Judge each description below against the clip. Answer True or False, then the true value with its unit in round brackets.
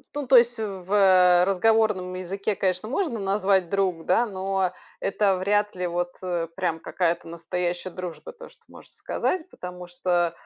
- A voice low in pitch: False (185 Hz)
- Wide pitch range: False (2.7 semitones)